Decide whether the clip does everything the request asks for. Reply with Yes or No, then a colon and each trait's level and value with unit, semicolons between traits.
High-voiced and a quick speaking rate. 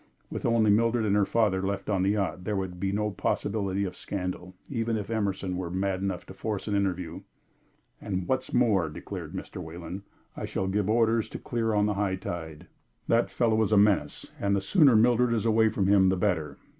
No: low, 100 Hz; fast, 210 wpm